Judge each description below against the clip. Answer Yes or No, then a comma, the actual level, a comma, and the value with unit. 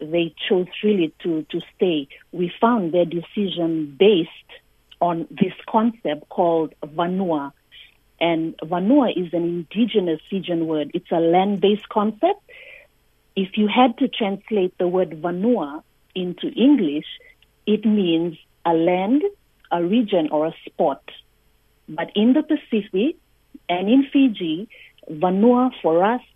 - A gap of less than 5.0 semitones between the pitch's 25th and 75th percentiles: No, wide, 5.6 semitones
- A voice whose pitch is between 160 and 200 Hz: Yes, medium, 185 Hz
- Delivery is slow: Yes, slow, 130 wpm